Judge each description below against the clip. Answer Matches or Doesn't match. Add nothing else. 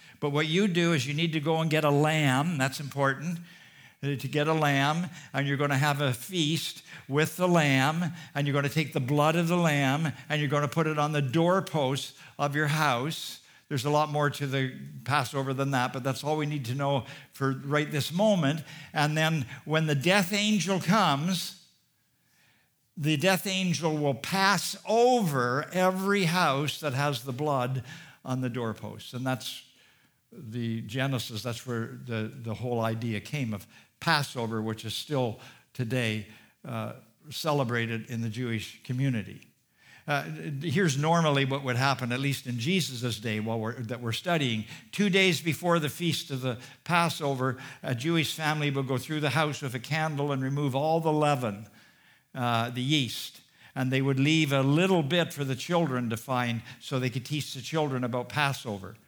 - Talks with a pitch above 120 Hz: Matches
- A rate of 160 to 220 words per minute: Matches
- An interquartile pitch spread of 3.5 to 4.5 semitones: Matches